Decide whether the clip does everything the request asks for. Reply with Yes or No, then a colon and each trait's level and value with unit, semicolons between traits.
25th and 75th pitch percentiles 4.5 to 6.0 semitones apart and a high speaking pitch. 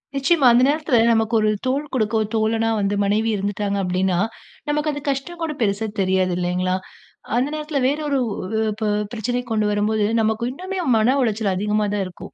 Yes: average, 5.1 semitones; high, 220 Hz